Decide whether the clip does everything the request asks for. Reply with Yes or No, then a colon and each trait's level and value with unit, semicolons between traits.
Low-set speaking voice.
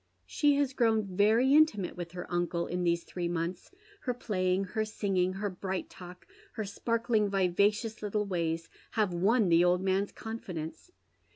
No: high, 195 Hz